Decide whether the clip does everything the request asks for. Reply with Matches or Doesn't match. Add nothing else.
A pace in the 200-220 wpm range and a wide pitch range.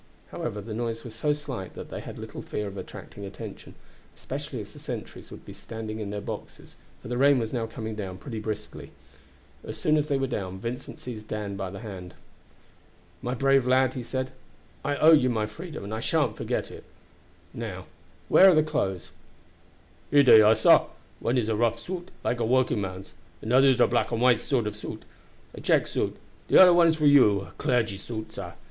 Doesn't match